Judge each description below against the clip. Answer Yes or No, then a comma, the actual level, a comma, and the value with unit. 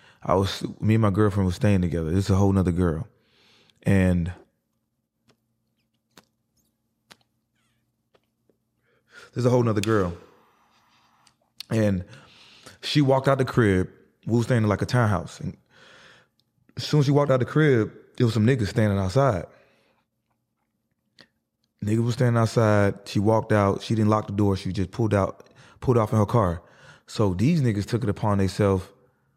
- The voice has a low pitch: Yes, low, 110 Hz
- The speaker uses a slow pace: No, average, 160 wpm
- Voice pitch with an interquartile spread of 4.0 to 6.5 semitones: No, average, 3.3 semitones